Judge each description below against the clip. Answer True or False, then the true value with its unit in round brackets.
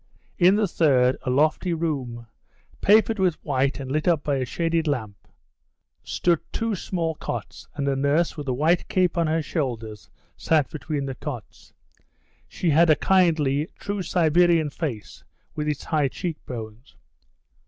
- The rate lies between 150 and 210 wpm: True (155 wpm)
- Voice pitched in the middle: True (155 Hz)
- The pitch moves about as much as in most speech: True (4.1 semitones)